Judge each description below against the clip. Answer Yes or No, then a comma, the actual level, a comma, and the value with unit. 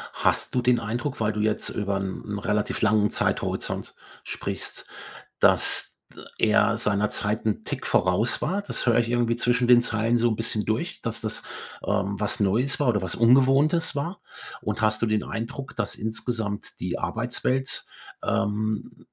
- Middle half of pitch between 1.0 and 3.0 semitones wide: Yes, average, 2.7 semitones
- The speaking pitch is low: Yes, low, 115 Hz